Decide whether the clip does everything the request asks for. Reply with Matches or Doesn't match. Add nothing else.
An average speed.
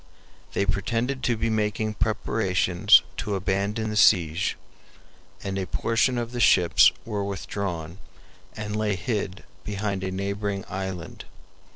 Doesn't match